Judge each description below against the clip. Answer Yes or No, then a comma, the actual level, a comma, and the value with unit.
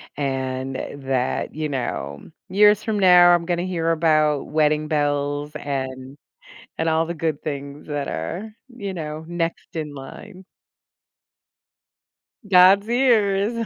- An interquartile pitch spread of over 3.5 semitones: Yes, average, 4.5 semitones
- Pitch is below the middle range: No, medium, 155 Hz